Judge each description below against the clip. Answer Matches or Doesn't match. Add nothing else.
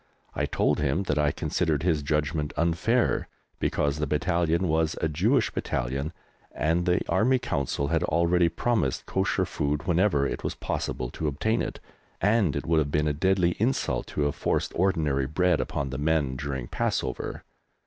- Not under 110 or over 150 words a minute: Doesn't match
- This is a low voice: Matches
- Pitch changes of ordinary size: Matches